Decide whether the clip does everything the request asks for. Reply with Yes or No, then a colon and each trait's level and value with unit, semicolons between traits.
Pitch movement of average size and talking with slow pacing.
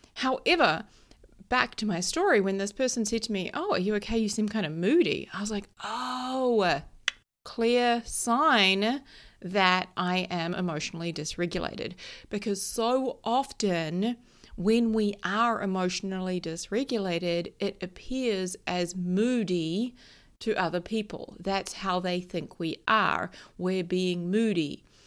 Yes: average, 4.1 semitones; slow, 130 wpm